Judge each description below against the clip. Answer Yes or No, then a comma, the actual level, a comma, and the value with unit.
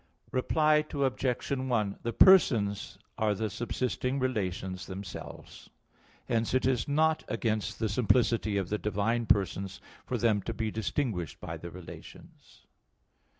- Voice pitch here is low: Yes, low, 110 Hz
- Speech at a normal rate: No, slow, 130 wpm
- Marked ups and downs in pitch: No, average, 4.3 semitones